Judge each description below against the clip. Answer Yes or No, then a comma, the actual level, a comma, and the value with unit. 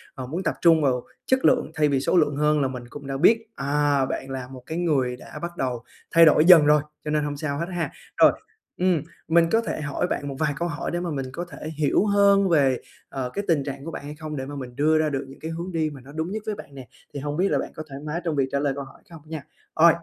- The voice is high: No, medium, 150 Hz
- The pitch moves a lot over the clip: No, average, 3.4 semitones